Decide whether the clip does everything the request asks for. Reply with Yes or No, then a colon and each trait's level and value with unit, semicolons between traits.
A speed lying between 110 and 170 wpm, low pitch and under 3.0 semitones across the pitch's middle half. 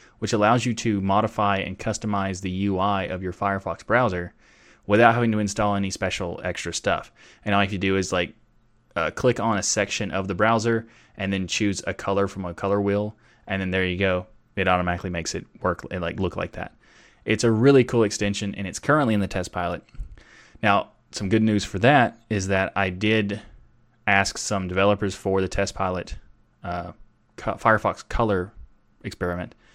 No: average, 190 wpm; low, 100 Hz; narrow, 2.5 semitones